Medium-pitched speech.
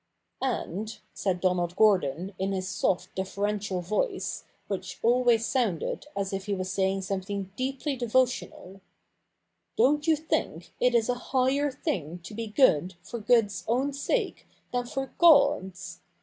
No: high, 210 Hz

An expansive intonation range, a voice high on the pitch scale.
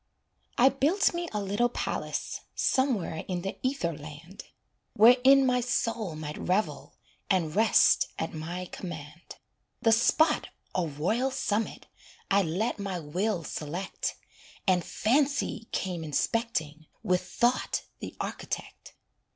Yes: wide, 6.4 semitones; high, 200 Hz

